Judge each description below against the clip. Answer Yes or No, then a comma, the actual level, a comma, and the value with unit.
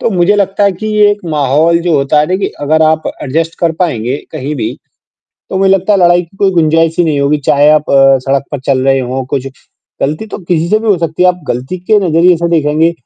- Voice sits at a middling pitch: Yes, medium, 165 Hz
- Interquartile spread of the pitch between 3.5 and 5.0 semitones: Yes, average, 3.8 semitones